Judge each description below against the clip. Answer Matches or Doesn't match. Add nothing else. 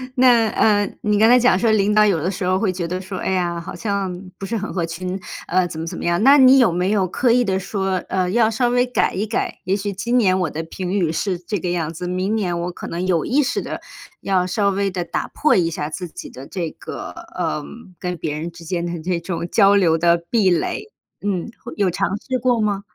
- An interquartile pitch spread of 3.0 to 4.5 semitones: Matches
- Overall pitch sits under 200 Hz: Matches